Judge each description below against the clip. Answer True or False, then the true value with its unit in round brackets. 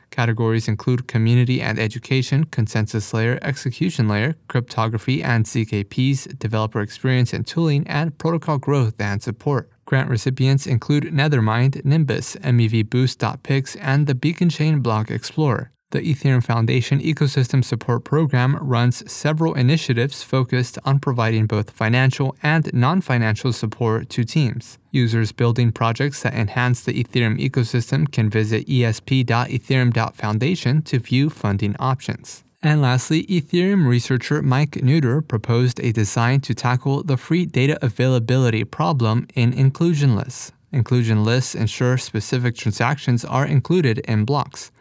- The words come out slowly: True (125 wpm)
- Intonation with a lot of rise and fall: False (3.4 semitones)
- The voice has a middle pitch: False (125 Hz)